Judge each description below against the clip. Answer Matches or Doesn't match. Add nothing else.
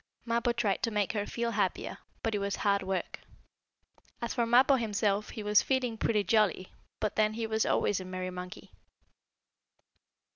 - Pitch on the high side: Matches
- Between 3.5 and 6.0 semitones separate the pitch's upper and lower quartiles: Doesn't match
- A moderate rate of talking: Matches